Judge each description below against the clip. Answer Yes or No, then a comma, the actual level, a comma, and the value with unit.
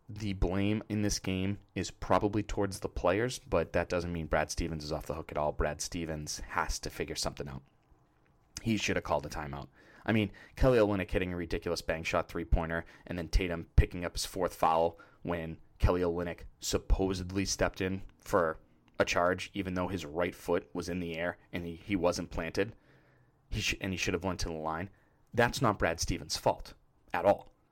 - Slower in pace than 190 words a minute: No, fast, 205 wpm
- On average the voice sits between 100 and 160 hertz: No, very low, 90 Hz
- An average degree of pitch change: Yes, average, 3.4 semitones